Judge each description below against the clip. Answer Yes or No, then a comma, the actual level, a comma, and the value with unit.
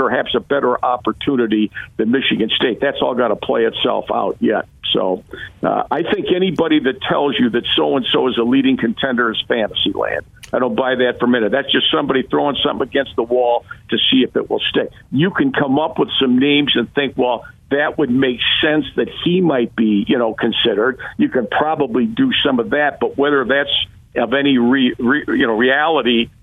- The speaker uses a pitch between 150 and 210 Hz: No, low, 130 Hz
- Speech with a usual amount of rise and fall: Yes, average, 3.1 semitones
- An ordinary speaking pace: No, fast, 210 wpm